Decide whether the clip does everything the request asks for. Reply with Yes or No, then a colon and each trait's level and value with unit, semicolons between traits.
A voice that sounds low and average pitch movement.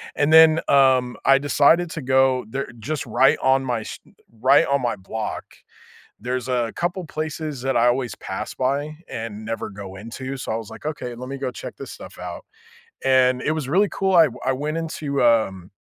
Yes: low, 130 Hz; average, 3.6 semitones